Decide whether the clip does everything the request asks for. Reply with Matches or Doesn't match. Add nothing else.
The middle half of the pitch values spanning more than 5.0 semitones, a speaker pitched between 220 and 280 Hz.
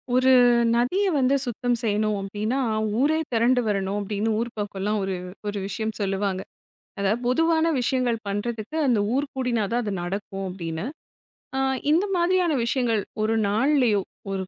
Doesn't match